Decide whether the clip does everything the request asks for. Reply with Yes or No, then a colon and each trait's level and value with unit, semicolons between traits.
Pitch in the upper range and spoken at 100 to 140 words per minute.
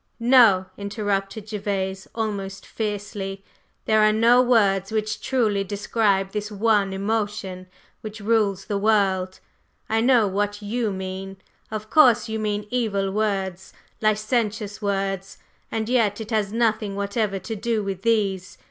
Yes: high, 205 Hz; slow, 135 wpm